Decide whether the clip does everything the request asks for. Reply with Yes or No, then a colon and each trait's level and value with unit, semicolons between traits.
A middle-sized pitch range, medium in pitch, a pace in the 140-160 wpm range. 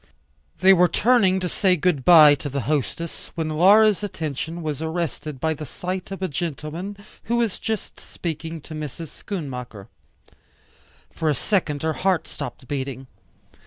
Yes: average, 4.0 semitones; medium, 160 Hz; average, 155 wpm